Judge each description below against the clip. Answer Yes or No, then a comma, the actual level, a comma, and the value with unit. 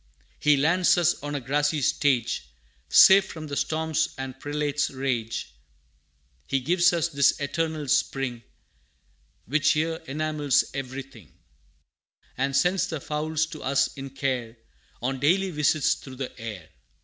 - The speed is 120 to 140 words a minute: Yes, slow, 135 wpm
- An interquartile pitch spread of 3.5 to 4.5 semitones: No, average, 2.9 semitones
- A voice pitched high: No, medium, 145 Hz